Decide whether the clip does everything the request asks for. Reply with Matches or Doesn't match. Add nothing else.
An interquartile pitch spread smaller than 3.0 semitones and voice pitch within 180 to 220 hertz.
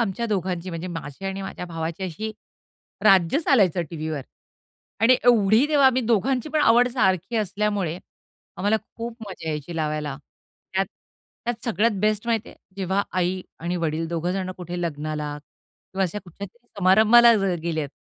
Doesn't match